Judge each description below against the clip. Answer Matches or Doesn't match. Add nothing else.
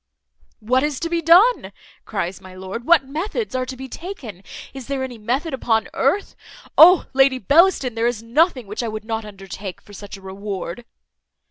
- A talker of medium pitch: Doesn't match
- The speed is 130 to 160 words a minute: Doesn't match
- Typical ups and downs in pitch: Doesn't match